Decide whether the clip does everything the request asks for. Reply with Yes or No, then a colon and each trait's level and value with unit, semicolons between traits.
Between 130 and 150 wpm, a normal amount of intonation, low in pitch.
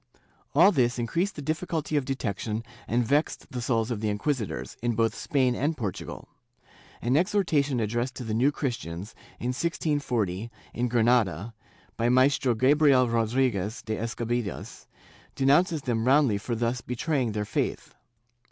Yes: average, 145 wpm; average, 3.9 semitones; low, 125 Hz